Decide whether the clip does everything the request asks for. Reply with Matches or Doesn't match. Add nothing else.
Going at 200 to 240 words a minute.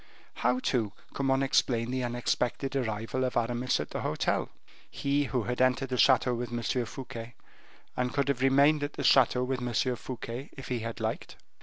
Doesn't match